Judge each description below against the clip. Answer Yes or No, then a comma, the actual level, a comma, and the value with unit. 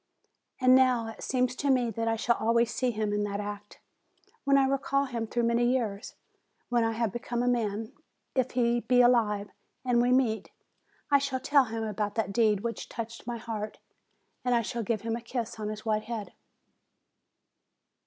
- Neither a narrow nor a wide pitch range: No, narrow, 2.3 semitones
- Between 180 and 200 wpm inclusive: Yes, average, 190 wpm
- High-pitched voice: Yes, high, 235 Hz